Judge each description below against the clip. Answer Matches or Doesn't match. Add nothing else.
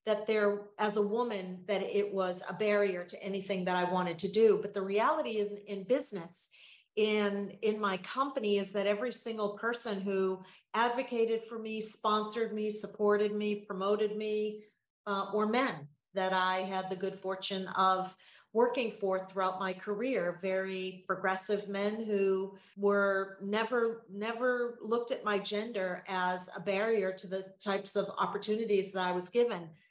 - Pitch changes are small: Matches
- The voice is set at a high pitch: Matches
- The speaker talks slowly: Doesn't match